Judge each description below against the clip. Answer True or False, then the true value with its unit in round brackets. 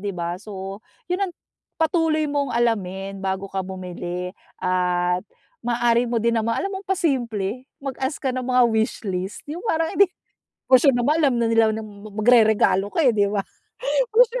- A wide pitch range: True (5.9 semitones)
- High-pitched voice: True (225 Hz)